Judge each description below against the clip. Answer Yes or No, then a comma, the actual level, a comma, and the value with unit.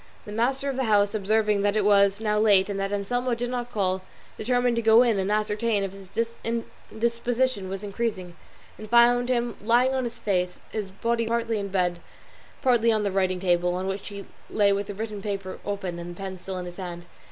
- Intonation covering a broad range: No, average, 3.2 semitones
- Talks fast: Yes, fast, 215 wpm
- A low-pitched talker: No, high, 210 Hz